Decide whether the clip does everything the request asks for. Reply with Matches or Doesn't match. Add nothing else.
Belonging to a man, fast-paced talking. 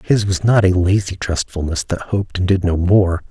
Matches